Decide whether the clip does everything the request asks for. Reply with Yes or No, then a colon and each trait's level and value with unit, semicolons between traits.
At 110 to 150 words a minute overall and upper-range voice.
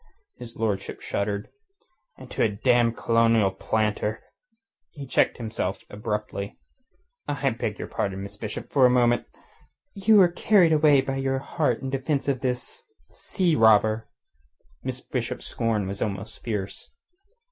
No: average, 140 wpm; low, 115 Hz